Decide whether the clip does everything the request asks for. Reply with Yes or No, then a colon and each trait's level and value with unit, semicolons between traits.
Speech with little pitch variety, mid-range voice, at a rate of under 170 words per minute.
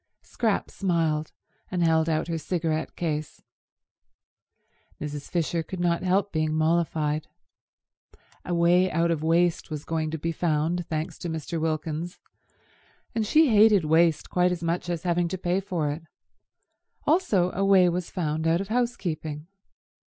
Yes: narrow, 2.3 semitones; medium, 170 Hz; average, 150 wpm